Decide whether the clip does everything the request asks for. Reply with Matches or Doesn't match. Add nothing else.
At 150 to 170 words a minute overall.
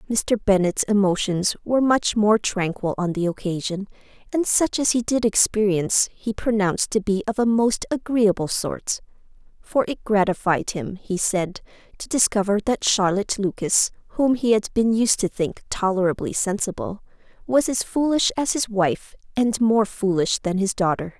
Matches